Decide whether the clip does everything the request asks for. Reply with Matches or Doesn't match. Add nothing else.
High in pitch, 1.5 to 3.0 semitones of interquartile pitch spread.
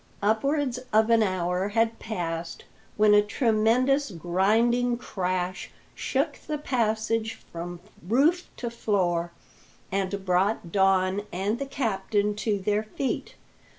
Doesn't match